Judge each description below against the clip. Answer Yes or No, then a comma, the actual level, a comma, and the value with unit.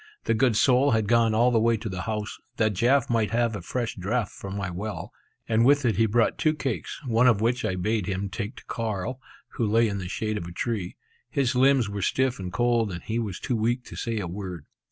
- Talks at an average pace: No, fast, 240 wpm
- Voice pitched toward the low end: Yes, low, 110 Hz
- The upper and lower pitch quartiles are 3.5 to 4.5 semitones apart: No, average, 3.1 semitones